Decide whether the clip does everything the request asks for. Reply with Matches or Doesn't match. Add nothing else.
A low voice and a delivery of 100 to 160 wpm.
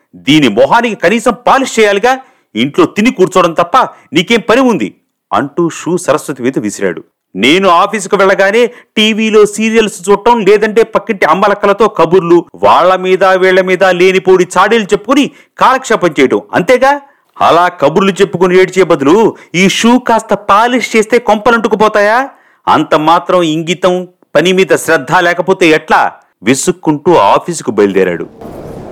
Doesn't match